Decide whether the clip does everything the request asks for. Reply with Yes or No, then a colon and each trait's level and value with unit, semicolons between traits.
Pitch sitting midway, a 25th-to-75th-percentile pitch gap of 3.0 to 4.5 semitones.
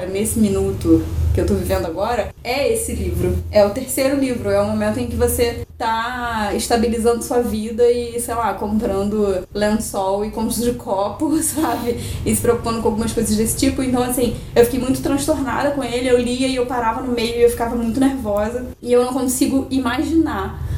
No: high, 235 Hz; average, 3.4 semitones